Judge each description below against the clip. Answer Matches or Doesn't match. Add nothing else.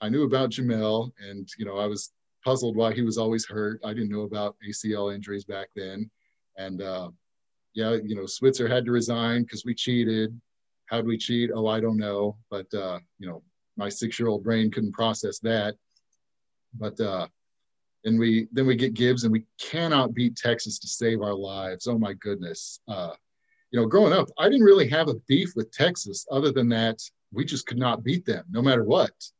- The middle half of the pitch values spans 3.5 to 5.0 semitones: Doesn't match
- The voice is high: Doesn't match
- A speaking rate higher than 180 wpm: Matches